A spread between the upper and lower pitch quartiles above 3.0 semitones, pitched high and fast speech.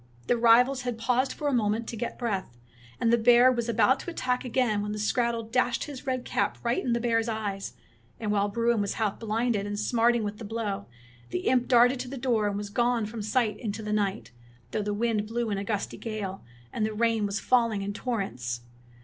No: narrow, 2.6 semitones; high, 225 Hz; fast, 225 wpm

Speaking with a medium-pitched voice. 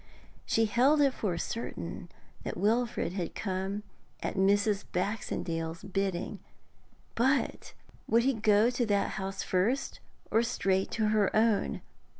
No: high, 210 Hz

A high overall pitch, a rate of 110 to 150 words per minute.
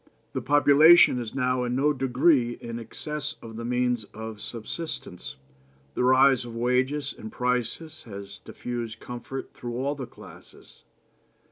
No: low, 125 Hz; slow, 135 wpm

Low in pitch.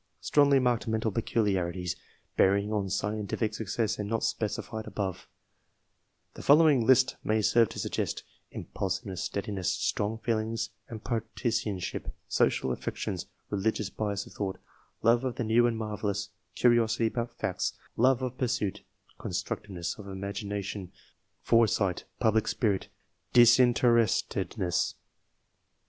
Yes: low, 110 Hz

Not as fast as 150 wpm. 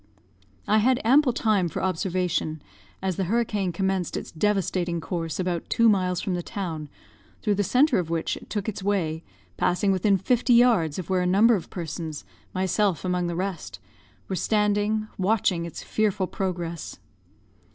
No: average, 160 wpm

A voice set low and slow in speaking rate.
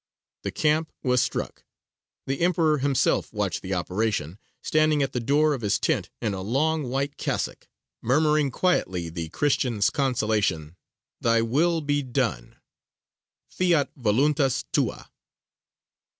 Yes: low, 130 Hz; slow, 125 wpm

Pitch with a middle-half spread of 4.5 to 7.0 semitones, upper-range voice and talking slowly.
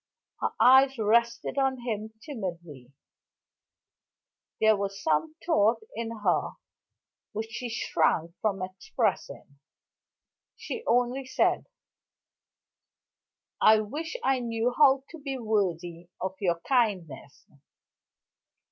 Yes: wide, 5.4 semitones; high, 220 Hz; slow, 100 wpm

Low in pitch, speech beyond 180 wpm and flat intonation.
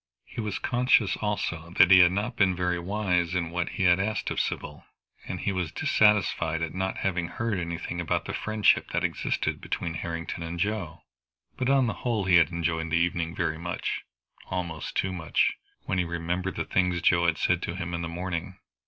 Yes: very low, 90 Hz; average, 200 wpm; narrow, 2.2 semitones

